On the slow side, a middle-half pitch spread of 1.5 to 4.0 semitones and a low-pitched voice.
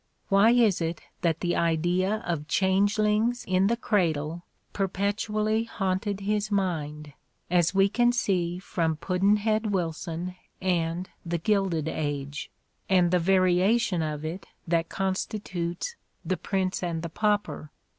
No: slow, 125 wpm; average, 3.6 semitones; medium, 185 Hz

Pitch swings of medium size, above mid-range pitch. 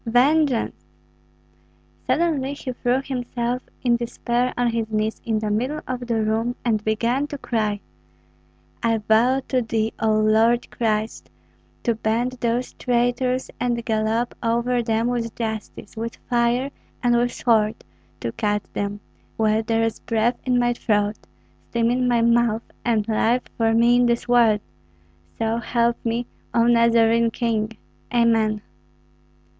No: narrow, 1.8 semitones; high, 235 Hz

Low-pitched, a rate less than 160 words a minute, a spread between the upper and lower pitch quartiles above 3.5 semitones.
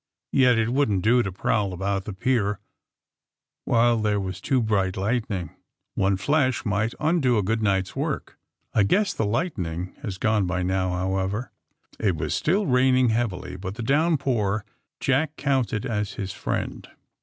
No: low, 110 Hz; average, 165 wpm; average, 4.8 semitones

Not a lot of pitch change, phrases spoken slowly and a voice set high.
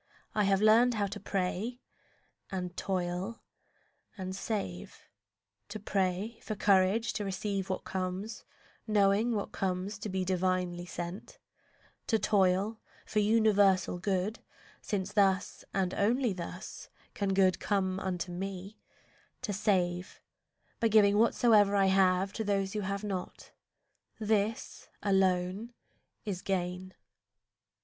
Yes: narrow, 2.3 semitones; slow, 120 wpm; high, 195 Hz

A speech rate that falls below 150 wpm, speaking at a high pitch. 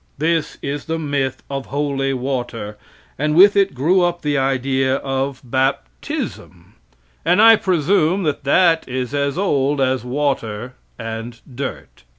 No: average, 140 wpm; medium, 140 Hz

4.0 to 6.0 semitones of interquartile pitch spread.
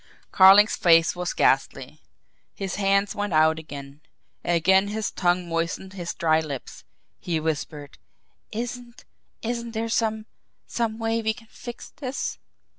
Yes: wide, 5.6 semitones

